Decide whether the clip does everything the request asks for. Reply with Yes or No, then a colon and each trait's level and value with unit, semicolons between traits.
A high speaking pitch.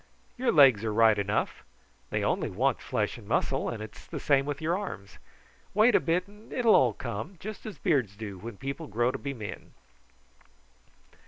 No: low, 135 Hz